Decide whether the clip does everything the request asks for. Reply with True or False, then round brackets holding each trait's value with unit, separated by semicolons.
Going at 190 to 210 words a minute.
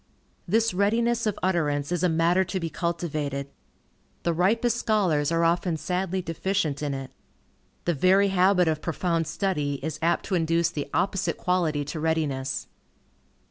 False (150 wpm)